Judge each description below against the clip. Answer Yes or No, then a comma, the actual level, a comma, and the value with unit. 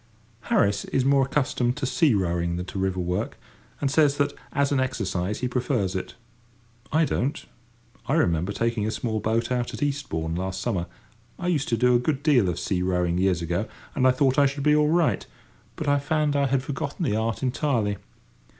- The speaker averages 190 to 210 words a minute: Yes, average, 200 wpm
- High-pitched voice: No, low, 125 Hz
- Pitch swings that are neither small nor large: No, wide, 6.8 semitones